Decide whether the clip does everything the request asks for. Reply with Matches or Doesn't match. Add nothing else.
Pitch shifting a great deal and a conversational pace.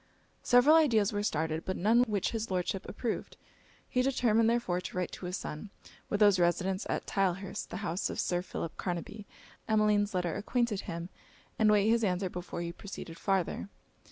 Doesn't match